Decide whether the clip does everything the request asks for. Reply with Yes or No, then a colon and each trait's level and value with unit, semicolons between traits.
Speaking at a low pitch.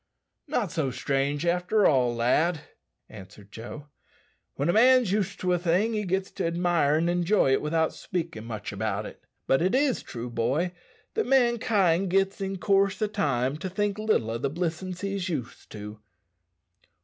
No: medium, 170 Hz